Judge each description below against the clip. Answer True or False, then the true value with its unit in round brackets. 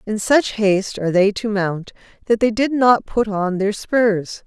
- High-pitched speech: True (210 Hz)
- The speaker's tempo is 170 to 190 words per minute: False (200 wpm)